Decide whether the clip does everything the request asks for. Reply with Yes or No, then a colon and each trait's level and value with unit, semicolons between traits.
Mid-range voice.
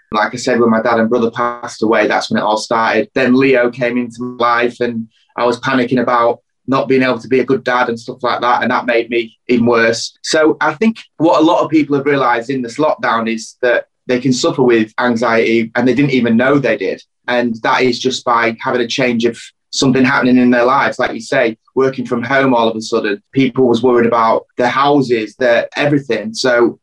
No: low, 120 Hz